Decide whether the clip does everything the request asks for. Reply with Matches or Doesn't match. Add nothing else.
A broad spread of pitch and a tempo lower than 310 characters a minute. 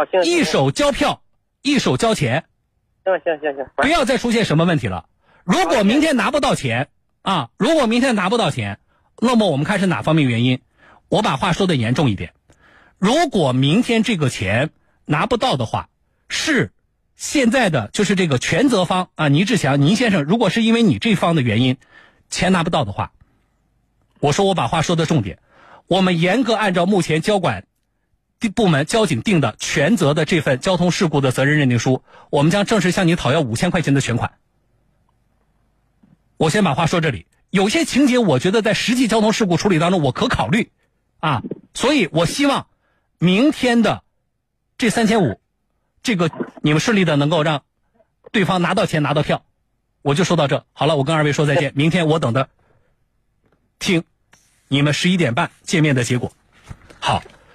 Matches